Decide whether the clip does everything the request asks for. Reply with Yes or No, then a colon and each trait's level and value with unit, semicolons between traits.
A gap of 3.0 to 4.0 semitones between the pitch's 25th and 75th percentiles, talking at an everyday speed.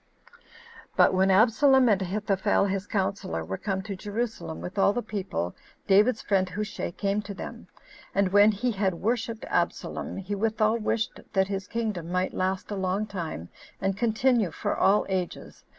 No: narrow, 2.4 semitones; average, 165 wpm